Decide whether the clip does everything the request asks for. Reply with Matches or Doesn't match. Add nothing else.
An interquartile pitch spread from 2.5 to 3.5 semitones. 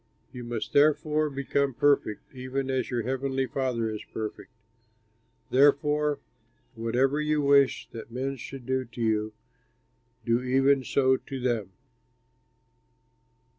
Matches